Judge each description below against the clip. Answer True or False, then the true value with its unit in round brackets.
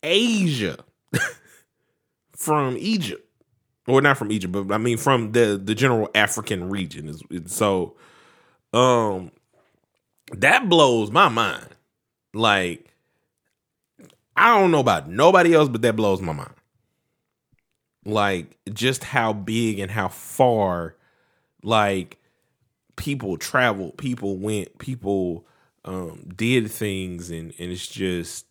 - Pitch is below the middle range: True (105 Hz)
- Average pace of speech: False (115 wpm)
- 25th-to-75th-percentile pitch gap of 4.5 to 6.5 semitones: True (4.9 semitones)